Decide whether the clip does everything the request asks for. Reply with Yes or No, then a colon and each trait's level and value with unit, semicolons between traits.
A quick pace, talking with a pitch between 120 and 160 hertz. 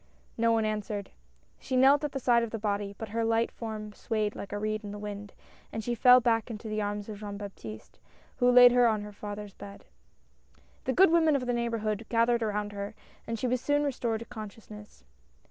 No: fast, 215 wpm; high, 220 Hz